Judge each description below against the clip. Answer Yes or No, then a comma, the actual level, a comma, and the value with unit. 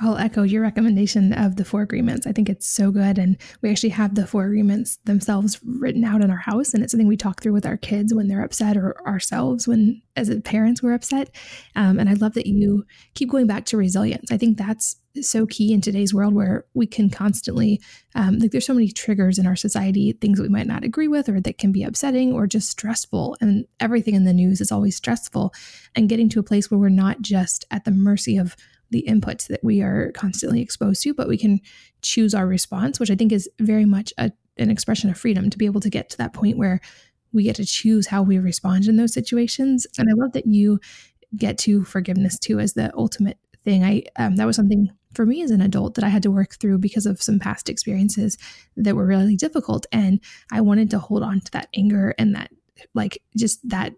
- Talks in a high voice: Yes, high, 210 Hz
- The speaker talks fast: Yes, fast, 230 wpm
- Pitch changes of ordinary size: No, narrow, 2.1 semitones